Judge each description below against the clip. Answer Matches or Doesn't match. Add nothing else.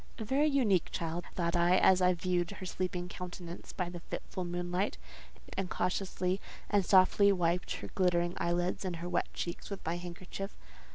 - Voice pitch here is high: Doesn't match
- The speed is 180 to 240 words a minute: Doesn't match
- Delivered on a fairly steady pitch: Matches